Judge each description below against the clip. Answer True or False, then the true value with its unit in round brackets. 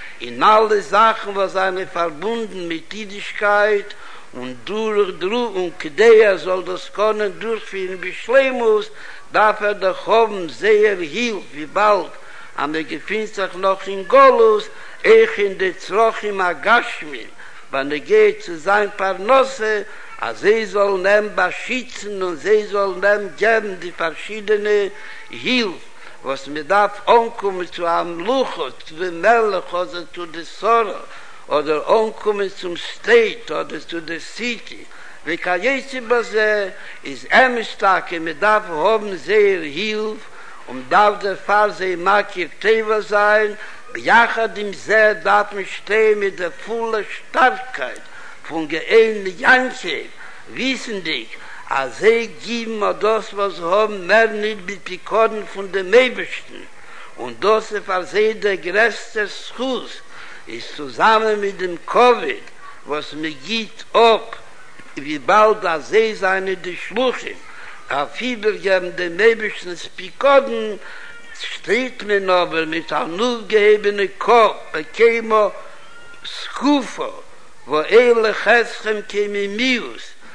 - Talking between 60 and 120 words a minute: False (130 wpm)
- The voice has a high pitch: True (210 Hz)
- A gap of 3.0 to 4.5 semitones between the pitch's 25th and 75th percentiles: True (4.0 semitones)